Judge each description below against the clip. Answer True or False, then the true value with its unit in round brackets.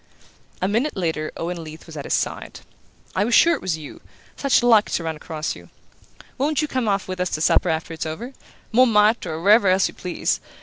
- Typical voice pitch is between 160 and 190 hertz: True (185 Hz)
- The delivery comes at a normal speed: False (215 wpm)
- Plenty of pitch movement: True (6.1 semitones)